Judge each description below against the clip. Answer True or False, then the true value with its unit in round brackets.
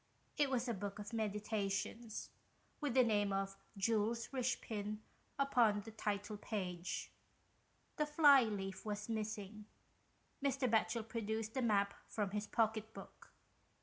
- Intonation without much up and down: True (2.3 semitones)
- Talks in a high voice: True (215 Hz)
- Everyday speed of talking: False (130 wpm)